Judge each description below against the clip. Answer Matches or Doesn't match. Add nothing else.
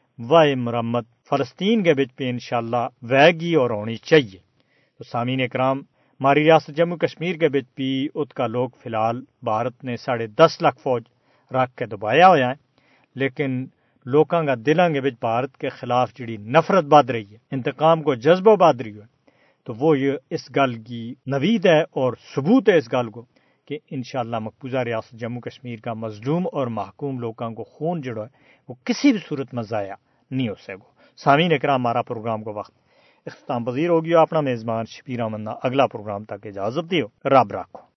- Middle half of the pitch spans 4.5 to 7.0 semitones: Doesn't match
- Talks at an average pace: Matches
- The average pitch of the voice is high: Doesn't match